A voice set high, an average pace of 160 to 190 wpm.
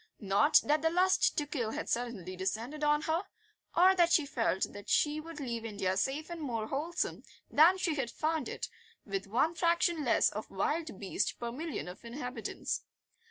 Yes: very high, 285 Hz; average, 180 wpm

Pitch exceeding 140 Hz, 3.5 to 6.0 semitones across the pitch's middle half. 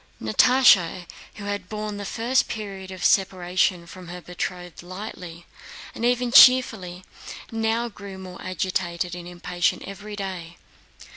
No: high, 190 Hz; average, 3.1 semitones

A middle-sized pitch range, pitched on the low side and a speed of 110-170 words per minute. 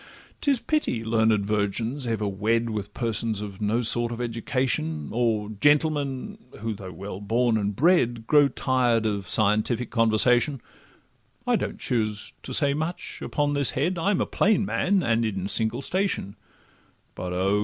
Yes: average, 4.6 semitones; low, 115 Hz; average, 155 wpm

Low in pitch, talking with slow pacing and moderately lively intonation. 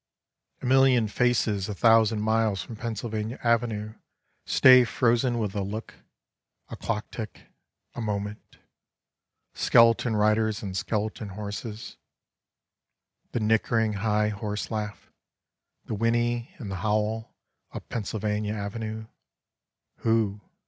No: low, 110 Hz; slow, 115 wpm; narrow, 1.7 semitones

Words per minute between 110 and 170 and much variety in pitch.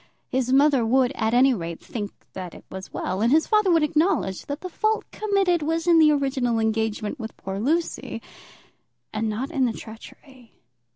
No: average, 180 wpm; wide, 6.1 semitones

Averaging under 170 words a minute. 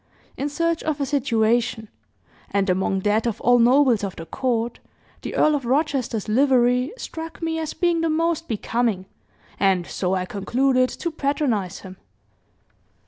Yes: average, 150 wpm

